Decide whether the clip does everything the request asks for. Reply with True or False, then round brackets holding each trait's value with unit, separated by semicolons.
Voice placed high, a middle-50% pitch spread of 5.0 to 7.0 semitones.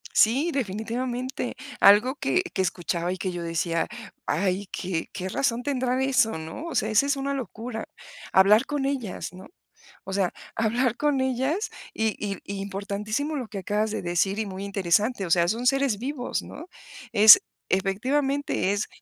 True (220 Hz; 5.3 semitones)